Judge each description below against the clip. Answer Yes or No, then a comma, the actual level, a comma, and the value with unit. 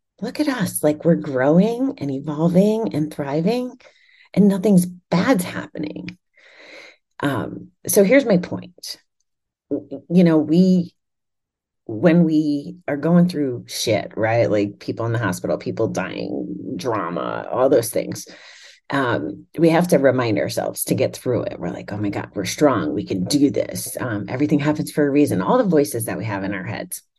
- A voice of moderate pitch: Yes, medium, 160 Hz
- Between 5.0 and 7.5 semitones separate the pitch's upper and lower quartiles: Yes, wide, 5.5 semitones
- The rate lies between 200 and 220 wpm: No, average, 170 wpm